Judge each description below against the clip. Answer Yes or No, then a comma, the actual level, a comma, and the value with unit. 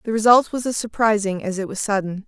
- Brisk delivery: Yes, fast, 235 wpm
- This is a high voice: Yes, high, 210 Hz